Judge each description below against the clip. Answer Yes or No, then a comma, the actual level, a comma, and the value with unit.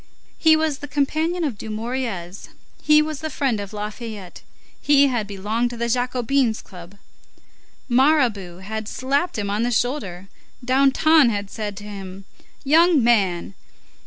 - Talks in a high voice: Yes, high, 235 Hz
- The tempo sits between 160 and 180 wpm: No, average, 140 wpm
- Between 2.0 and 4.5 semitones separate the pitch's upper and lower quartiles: No, wide, 5.4 semitones